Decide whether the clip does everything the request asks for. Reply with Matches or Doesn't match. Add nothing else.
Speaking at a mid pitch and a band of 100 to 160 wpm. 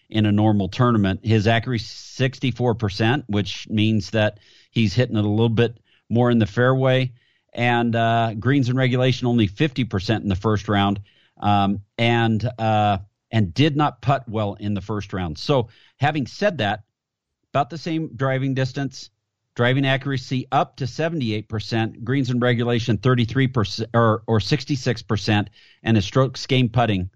Doesn't match